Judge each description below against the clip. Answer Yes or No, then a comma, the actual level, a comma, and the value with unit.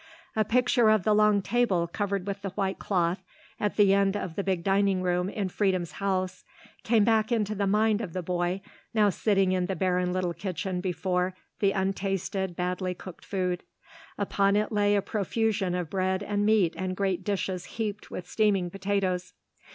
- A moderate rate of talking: Yes, average, 180 wpm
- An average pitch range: No, narrow, 2.1 semitones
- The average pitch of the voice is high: Yes, high, 195 Hz